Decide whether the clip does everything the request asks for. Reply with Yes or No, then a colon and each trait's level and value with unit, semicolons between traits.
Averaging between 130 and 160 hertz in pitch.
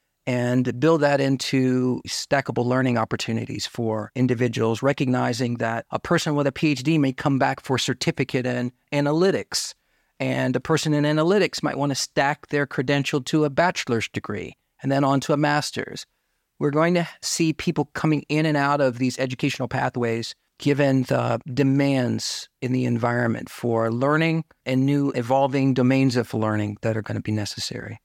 Yes: low, 135 Hz